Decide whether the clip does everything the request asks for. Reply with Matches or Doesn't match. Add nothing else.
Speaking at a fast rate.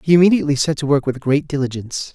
Matches